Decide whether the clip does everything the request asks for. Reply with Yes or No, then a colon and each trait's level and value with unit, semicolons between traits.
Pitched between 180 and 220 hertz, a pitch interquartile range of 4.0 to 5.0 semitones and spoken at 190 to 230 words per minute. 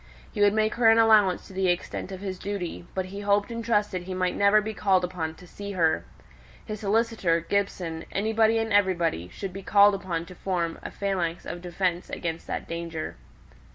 No: high, 190 Hz; average, 2.8 semitones; average, 195 wpm